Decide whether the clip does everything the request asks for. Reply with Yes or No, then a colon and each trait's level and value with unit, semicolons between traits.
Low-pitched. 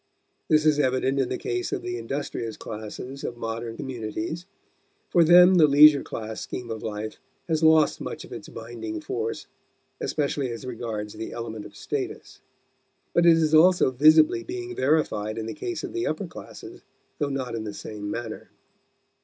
Yes: low, 130 Hz